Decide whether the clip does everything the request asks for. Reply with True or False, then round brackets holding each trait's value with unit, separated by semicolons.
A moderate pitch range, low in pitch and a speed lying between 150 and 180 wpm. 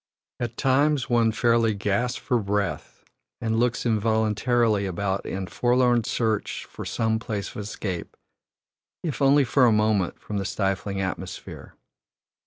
False (3.2 semitones; 110 Hz; 135 wpm)